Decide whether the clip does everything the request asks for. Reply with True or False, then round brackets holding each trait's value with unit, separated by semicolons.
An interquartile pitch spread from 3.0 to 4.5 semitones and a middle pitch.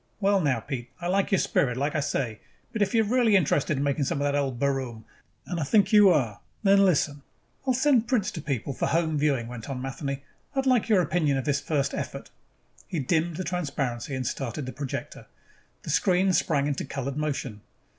False (5.5 semitones; 145 Hz)